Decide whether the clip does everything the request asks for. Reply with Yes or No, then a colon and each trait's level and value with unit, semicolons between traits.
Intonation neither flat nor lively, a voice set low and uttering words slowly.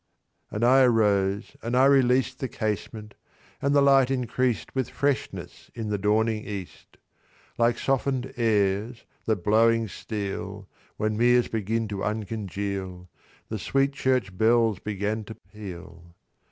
Yes: average, 3.5 semitones; low, 110 Hz; slow, 130 wpm